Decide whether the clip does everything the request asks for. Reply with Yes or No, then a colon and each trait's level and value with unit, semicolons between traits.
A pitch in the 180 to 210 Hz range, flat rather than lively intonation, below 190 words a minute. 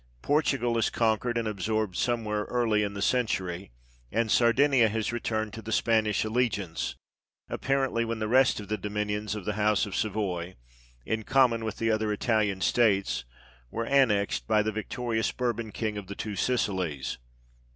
No: low, 110 Hz; narrow, 2.2 semitones; average, 160 wpm